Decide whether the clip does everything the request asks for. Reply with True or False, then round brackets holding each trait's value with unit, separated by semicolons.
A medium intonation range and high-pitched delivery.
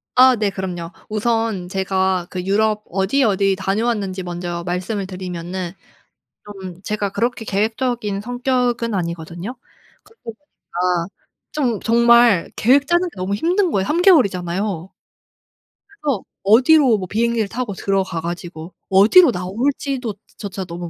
True (4.6 semitones; 205 Hz)